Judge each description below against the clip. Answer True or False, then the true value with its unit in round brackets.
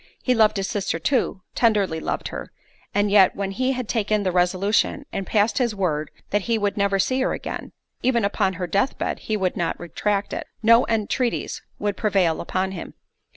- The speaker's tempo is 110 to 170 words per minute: False (185 wpm)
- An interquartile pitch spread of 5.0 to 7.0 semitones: False (3.0 semitones)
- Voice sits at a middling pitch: False (205 Hz)